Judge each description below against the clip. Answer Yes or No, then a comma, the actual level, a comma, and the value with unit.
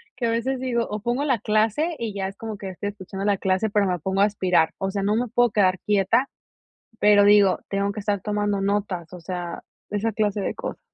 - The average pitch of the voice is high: Yes, high, 205 Hz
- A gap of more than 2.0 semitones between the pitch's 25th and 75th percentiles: Yes, narrow, 2.5 semitones